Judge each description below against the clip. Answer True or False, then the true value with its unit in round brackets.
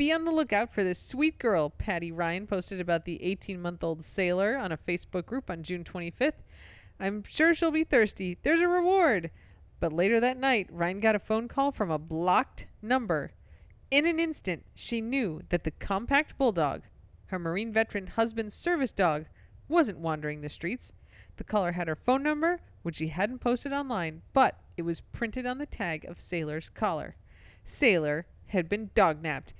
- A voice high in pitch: True (195 Hz)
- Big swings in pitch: True (7.2 semitones)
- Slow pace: False (180 wpm)